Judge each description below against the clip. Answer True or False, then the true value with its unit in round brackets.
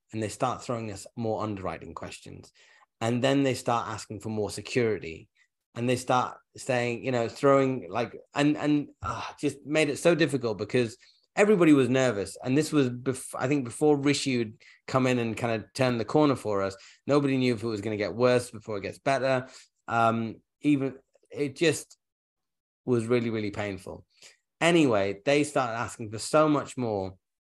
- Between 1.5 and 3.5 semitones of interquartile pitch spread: False (4.0 semitones)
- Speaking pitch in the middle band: False (125 Hz)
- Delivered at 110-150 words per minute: False (185 wpm)